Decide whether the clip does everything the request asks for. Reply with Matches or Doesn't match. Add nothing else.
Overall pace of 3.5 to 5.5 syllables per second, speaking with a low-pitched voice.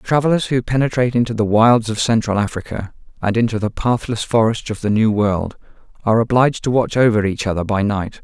Doesn't match